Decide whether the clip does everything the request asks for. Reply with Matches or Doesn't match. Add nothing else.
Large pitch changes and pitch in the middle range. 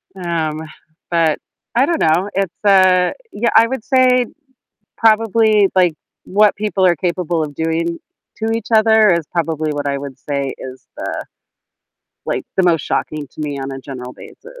Matches